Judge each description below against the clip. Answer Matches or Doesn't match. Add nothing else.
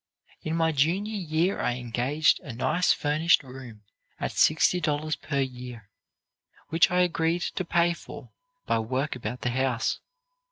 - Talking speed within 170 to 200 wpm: Doesn't match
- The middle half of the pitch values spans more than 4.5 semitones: Matches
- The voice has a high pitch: Doesn't match